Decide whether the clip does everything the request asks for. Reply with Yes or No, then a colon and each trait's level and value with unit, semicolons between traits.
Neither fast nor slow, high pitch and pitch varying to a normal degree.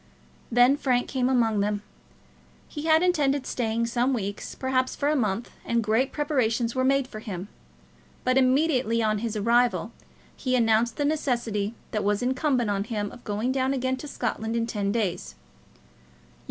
Yes: average, 165 wpm; high, 240 Hz; average, 3.2 semitones